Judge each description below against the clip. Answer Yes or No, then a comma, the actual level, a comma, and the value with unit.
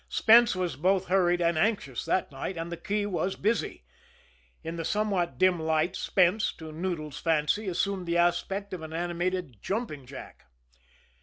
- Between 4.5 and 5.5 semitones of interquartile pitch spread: No, average, 3.2 semitones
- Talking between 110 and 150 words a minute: No, average, 160 wpm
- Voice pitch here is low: No, medium, 175 Hz